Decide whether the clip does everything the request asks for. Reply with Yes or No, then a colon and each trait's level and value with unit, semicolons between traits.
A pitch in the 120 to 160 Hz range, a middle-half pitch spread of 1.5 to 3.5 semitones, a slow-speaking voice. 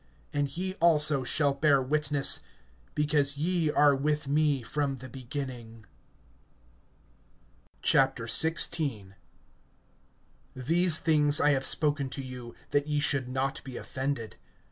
Yes: medium, 140 Hz; narrow, 2.4 semitones; slow, 115 wpm